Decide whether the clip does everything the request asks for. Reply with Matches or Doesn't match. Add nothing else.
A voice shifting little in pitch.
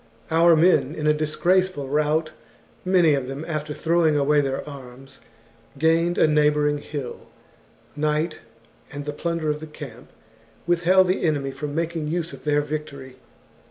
Matches